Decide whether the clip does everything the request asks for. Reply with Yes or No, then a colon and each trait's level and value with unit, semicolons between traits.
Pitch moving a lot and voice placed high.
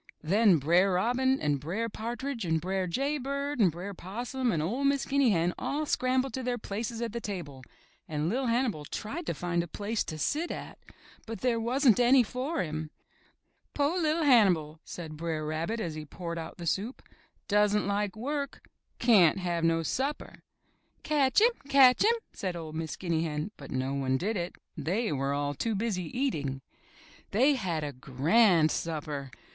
Yes: wide, 7.7 semitones; high, 200 Hz